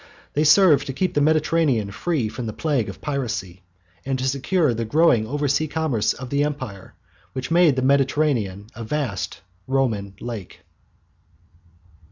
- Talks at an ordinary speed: Yes, average, 155 wpm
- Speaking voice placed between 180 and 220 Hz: No, low, 135 Hz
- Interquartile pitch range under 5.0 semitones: No, wide, 5.4 semitones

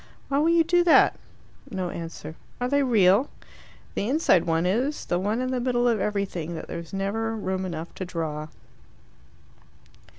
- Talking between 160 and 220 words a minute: Yes, average, 165 wpm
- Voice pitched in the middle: No, high, 200 Hz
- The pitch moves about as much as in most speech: No, wide, 6.5 semitones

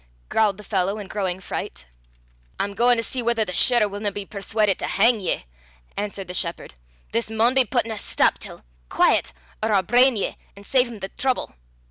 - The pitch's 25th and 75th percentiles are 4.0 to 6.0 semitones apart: No, average, 3.3 semitones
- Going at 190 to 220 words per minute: Yes, average, 195 wpm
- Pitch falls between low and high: No, high, 210 Hz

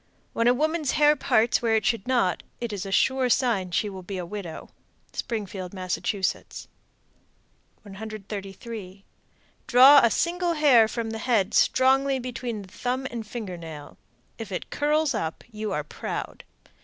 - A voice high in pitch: Yes, high, 225 Hz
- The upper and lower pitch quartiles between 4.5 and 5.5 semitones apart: Yes, average, 4.9 semitones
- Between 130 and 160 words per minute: Yes, average, 155 wpm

